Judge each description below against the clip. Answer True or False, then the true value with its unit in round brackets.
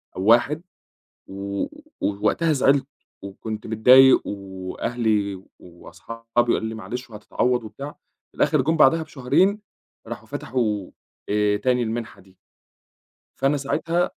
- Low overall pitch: True (115 Hz)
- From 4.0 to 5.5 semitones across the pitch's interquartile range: True (4.6 semitones)